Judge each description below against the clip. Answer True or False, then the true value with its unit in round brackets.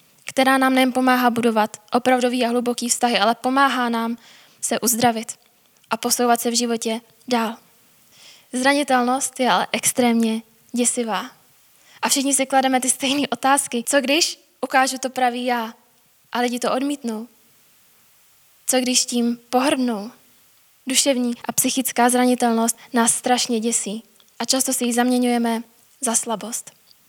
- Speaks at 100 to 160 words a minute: True (135 wpm)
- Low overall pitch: False (245 Hz)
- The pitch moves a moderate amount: False (1.8 semitones)